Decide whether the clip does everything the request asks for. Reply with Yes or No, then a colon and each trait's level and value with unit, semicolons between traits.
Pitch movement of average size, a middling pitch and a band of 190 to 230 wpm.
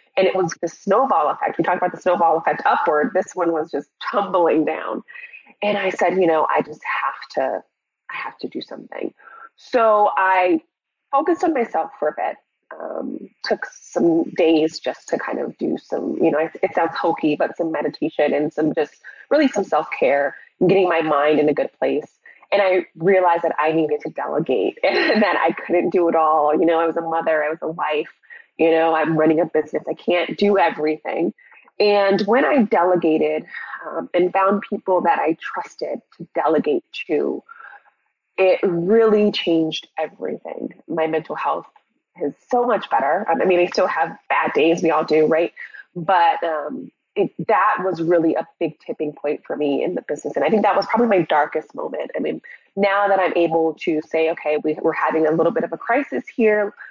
Yes: average, 4.3 semitones; medium, 170 Hz; average, 200 wpm